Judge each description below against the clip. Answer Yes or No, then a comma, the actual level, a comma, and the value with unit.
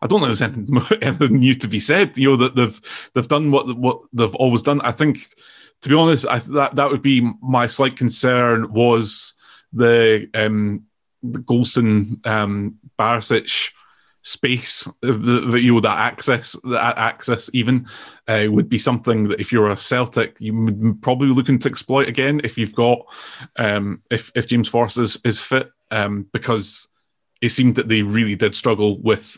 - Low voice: Yes, low, 120 Hz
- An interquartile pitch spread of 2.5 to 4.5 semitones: Yes, average, 2.8 semitones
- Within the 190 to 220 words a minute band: No, average, 180 wpm